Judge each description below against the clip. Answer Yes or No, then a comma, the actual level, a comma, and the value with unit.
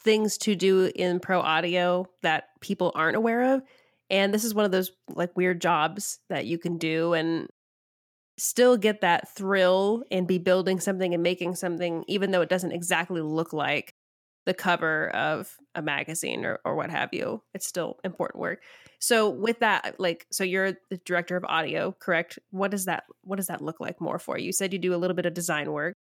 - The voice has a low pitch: No, medium, 180 Hz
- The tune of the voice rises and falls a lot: No, narrow, 2.4 semitones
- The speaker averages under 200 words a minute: No, fast, 205 wpm